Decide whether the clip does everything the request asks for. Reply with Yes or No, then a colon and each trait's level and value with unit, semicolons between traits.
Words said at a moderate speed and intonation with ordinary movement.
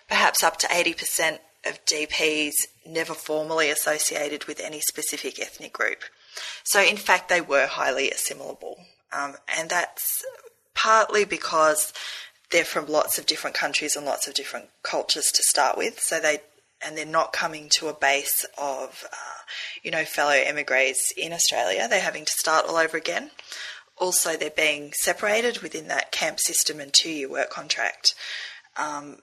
No: average, 160 wpm; narrow, 2.2 semitones